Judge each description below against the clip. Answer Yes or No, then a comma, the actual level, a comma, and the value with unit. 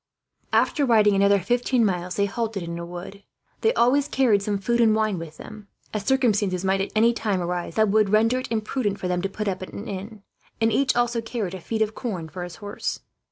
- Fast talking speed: Yes, fast, 225 wpm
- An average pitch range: Yes, average, 3.2 semitones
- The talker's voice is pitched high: Yes, high, 210 Hz